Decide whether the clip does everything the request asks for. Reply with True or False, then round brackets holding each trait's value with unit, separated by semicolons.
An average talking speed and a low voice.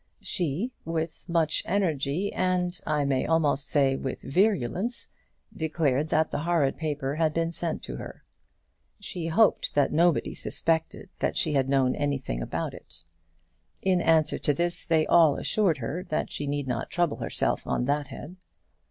False (160 wpm; 160 Hz)